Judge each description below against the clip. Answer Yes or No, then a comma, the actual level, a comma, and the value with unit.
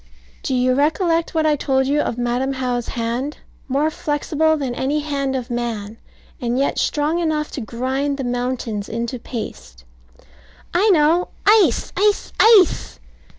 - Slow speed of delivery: No, average, 150 wpm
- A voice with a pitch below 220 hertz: No, very high, 270 Hz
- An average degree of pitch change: Yes, average, 4.1 semitones